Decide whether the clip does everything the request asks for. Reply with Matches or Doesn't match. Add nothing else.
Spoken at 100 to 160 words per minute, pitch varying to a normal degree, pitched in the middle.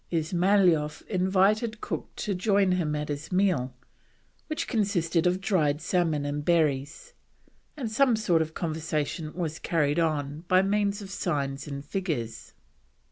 Matches